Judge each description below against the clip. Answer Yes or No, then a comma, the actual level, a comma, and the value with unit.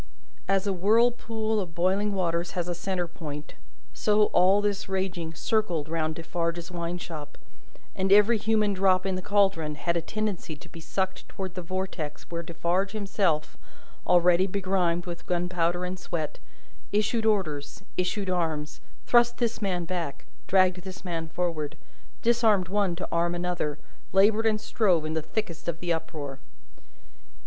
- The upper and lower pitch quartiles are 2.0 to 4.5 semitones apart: Yes, average, 3.0 semitones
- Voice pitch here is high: No, medium, 180 Hz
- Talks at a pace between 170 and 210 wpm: No, average, 155 wpm